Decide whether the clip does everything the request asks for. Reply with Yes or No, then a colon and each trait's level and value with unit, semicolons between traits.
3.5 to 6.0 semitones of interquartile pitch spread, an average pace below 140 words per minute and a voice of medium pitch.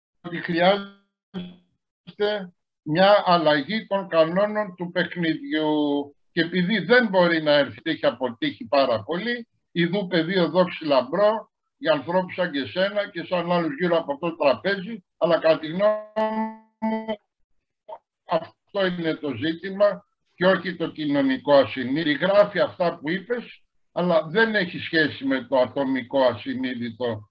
Yes: average, 4.9 semitones; average, 130 wpm; medium, 180 Hz